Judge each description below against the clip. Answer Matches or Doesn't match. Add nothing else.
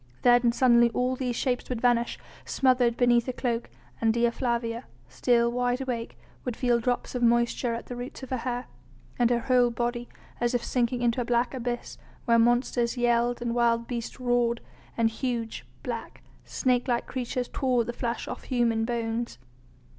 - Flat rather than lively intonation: Matches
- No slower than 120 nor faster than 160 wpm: Doesn't match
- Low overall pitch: Doesn't match